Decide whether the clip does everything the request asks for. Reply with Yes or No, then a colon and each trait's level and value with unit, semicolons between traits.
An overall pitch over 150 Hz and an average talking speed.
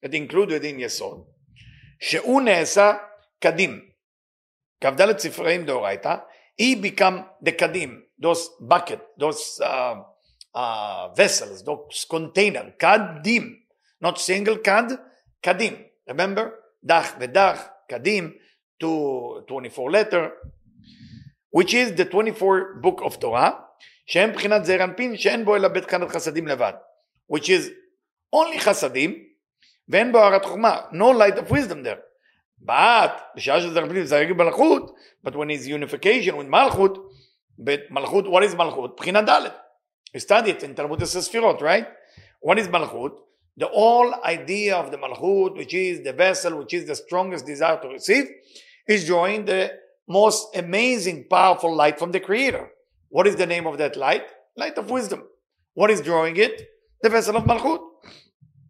No: high, 190 Hz; slow, 130 wpm